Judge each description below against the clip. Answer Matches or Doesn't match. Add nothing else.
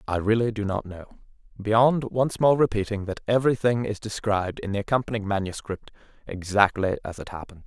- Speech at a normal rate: Matches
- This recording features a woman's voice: Doesn't match